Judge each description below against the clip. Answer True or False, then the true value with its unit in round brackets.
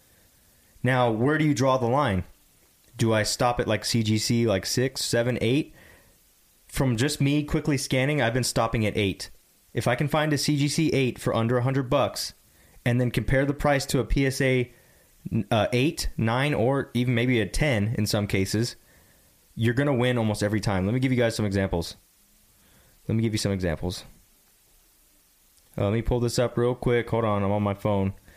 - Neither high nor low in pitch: False (120 Hz)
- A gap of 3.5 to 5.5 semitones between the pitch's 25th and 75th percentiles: True (4.1 semitones)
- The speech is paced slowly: False (190 wpm)